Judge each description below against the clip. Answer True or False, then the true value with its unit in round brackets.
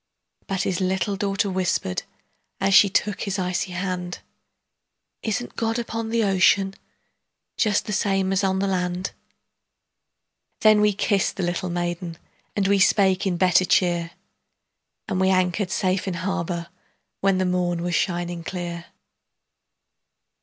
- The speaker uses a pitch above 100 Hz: True (190 Hz)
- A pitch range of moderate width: False (1.8 semitones)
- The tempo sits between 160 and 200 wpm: False (140 wpm)